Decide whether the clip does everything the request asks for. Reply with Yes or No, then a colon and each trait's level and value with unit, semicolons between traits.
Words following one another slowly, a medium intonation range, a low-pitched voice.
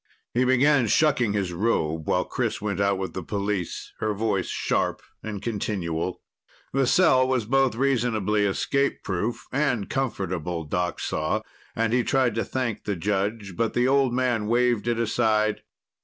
No: average, 155 wpm; average, 4.0 semitones; low, 110 Hz